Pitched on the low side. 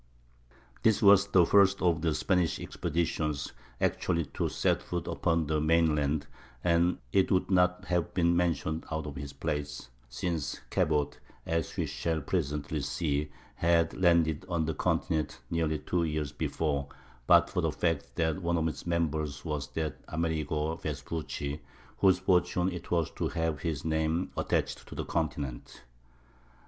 Yes: very low, 80 Hz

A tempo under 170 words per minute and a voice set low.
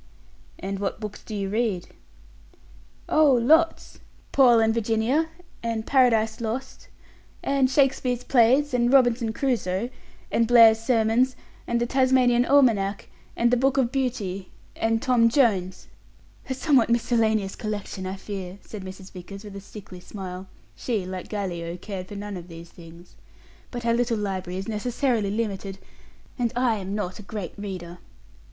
No: average, 150 wpm; high, 220 Hz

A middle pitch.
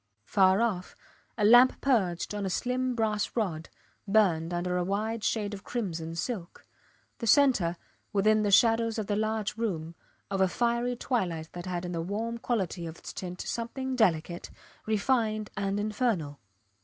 No: high, 205 Hz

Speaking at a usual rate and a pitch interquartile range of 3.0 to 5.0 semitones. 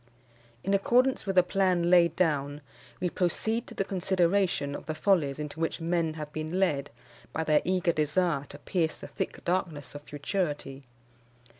Yes: average, 165 wpm; average, 3.9 semitones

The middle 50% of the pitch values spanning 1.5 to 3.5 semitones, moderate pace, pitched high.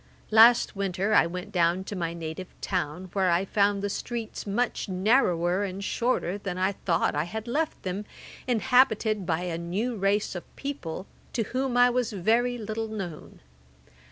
No: average, 3.9 semitones; average, 165 wpm; high, 200 Hz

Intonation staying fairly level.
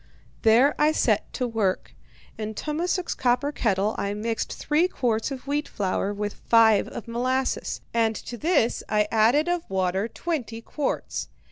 No: average, 5.1 semitones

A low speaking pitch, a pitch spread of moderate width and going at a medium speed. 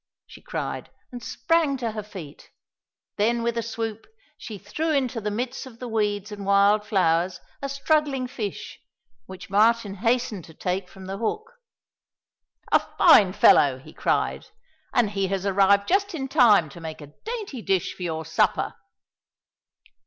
No: high, 210 Hz; average, 4.4 semitones; average, 160 wpm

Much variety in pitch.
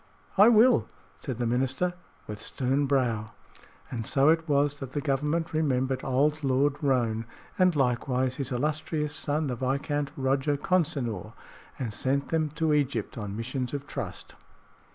No: average, 2.9 semitones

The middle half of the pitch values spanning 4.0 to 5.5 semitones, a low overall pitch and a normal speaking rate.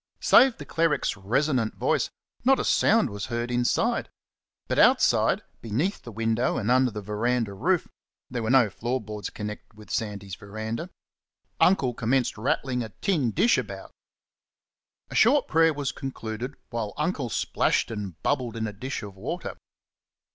Yes: average, 4.5 semitones; low, 120 Hz; average, 155 wpm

